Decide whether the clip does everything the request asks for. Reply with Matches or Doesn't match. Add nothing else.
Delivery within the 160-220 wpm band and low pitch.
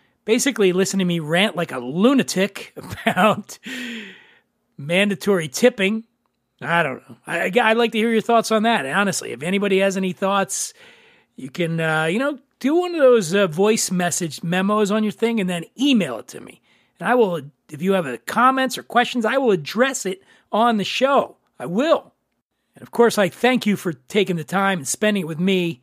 Doesn't match